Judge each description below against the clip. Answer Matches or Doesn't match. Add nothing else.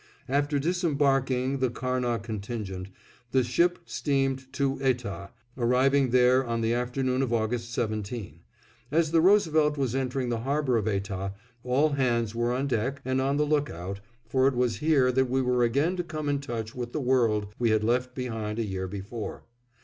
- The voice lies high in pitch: Doesn't match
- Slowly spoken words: Doesn't match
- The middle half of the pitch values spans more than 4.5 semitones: Doesn't match